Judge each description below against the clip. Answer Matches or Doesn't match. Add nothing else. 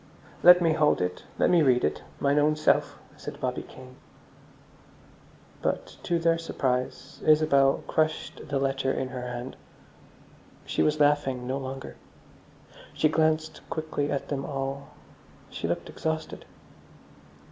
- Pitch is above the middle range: Doesn't match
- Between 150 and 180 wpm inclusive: Doesn't match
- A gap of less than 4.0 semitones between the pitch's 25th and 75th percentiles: Matches